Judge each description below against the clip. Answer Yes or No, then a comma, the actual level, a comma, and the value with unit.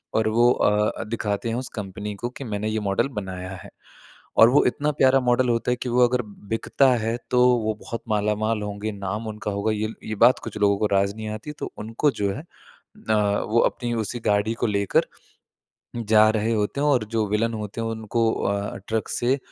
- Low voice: Yes, low, 110 Hz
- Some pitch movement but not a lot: No, narrow, 2.3 semitones